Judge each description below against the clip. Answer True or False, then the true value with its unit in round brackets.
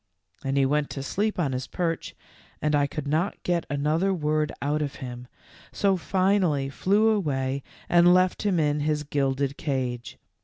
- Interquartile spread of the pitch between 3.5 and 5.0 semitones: True (4.3 semitones)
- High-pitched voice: False (150 Hz)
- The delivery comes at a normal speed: True (165 wpm)